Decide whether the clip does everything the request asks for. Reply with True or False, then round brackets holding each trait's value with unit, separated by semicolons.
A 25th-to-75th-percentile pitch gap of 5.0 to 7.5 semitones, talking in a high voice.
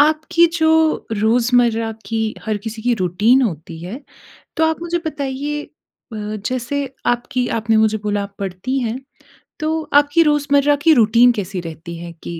True (5.5 semitones; 240 Hz)